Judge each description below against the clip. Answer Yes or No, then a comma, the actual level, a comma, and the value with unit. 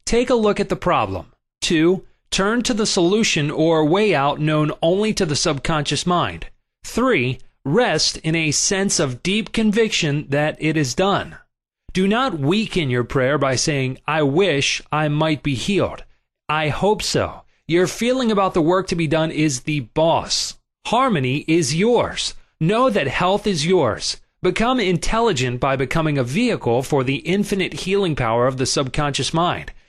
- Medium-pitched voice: Yes, medium, 160 Hz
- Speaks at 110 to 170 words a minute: Yes, average, 165 wpm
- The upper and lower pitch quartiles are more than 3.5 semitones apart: Yes, average, 5.2 semitones